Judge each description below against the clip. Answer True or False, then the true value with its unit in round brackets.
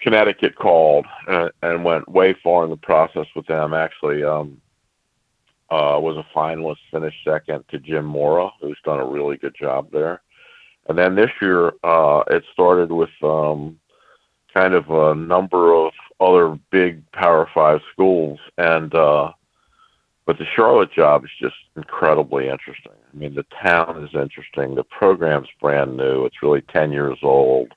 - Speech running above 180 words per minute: False (160 wpm)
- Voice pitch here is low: True (80 Hz)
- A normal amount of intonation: False (2.3 semitones)